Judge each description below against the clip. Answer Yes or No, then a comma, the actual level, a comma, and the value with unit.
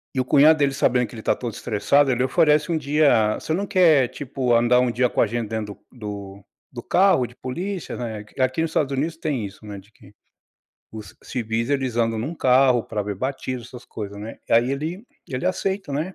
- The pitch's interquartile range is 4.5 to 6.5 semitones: Yes, average, 4.8 semitones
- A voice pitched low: Yes, low, 125 Hz